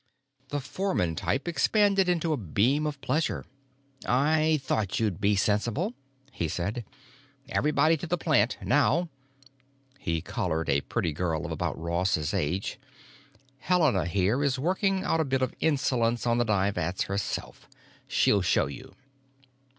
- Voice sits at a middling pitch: No, low, 120 Hz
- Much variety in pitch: Yes, wide, 8.7 semitones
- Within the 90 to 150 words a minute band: Yes, average, 145 wpm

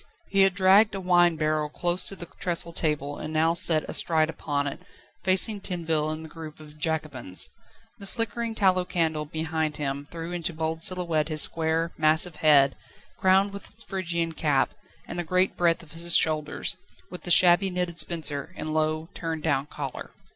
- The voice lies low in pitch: No, medium, 165 Hz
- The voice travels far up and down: No, narrow, 2.5 semitones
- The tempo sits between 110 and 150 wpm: No, average, 175 wpm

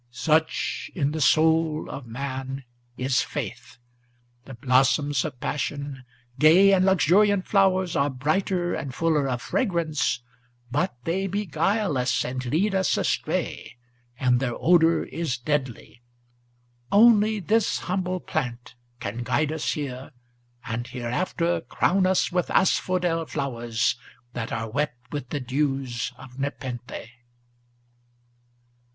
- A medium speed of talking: No, slow, 120 wpm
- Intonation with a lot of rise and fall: Yes, wide, 5.8 semitones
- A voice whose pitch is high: No, medium, 145 Hz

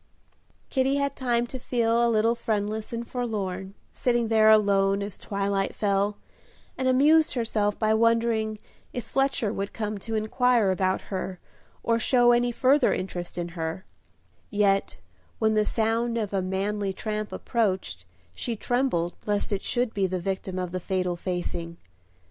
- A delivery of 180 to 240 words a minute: No, average, 155 wpm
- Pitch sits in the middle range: No, high, 215 Hz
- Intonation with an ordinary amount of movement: Yes, average, 3.5 semitones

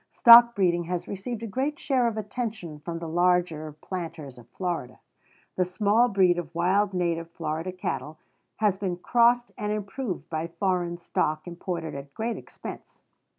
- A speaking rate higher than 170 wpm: No, average, 155 wpm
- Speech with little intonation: No, average, 4.0 semitones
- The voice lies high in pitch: No, medium, 180 Hz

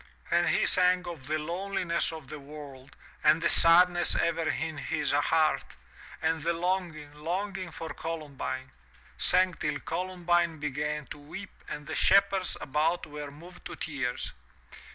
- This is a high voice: No, medium, 160 Hz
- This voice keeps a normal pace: Yes, average, 155 wpm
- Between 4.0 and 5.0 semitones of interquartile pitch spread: No, average, 2.9 semitones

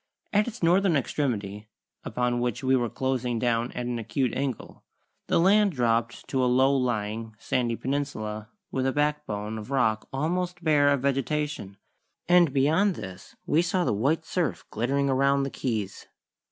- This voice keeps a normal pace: Yes, average, 160 wpm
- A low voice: Yes, low, 130 Hz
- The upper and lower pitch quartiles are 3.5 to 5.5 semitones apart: Yes, average, 4.5 semitones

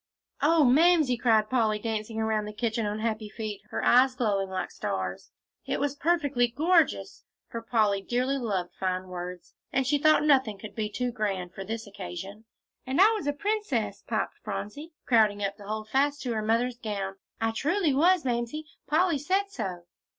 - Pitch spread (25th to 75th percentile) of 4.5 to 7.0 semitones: Yes, wide, 5.5 semitones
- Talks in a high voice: Yes, high, 230 Hz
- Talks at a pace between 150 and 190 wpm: Yes, average, 180 wpm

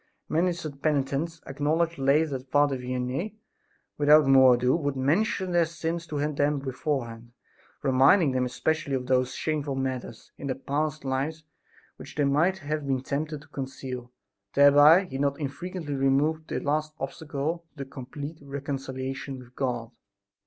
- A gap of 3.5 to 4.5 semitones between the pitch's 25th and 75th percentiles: No, average, 2.8 semitones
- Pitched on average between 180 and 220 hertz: No, medium, 140 Hz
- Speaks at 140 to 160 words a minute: Yes, average, 145 wpm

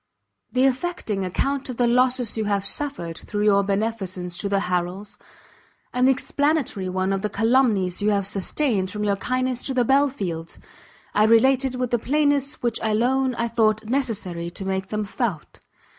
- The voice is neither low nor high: No, high, 220 Hz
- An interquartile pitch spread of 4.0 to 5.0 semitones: Yes, average, 4.7 semitones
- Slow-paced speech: No, average, 170 wpm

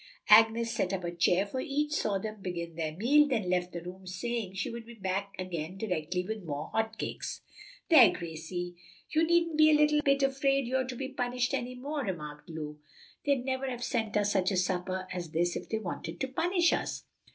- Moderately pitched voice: No, high, 215 Hz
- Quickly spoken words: Yes, fast, 210 wpm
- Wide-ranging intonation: Yes, wide, 6.6 semitones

